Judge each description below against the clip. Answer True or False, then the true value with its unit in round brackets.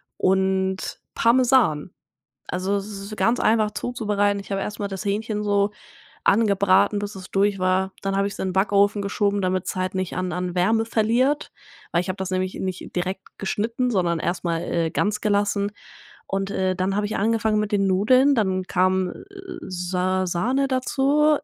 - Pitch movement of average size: False (2.3 semitones)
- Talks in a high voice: True (200 Hz)